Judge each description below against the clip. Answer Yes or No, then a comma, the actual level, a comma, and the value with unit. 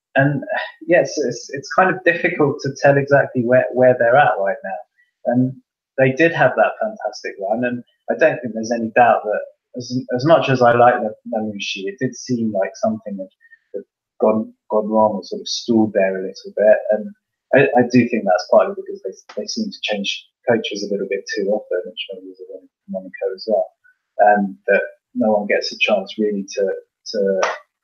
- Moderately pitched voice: No, low, 130 Hz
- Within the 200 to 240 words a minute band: Yes, fast, 205 wpm